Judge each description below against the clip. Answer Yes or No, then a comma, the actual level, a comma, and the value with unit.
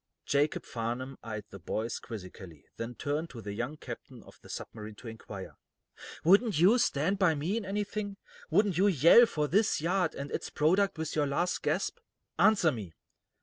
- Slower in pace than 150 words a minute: No, average, 175 wpm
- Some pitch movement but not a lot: No, wide, 8.8 semitones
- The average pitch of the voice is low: No, medium, 150 Hz